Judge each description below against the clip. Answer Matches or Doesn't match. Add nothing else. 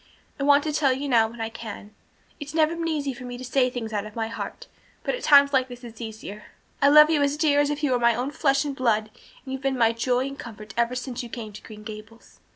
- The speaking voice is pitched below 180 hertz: Doesn't match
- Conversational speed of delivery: Doesn't match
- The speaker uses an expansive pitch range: Doesn't match